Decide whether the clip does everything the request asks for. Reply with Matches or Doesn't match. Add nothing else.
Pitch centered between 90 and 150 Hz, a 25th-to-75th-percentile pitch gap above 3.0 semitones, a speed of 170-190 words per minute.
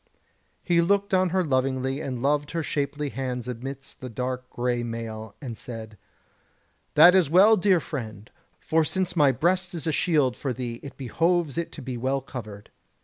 Matches